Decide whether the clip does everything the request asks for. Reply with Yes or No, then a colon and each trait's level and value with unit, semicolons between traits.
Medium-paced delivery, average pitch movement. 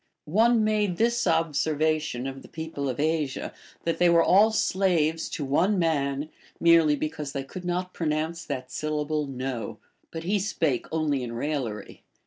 Yes: average, 155 wpm; average, 3.7 semitones